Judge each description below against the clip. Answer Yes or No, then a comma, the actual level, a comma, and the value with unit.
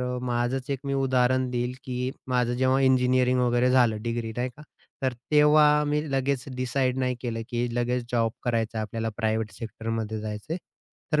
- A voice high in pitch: No, low, 125 Hz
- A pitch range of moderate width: No, narrow, 2.0 semitones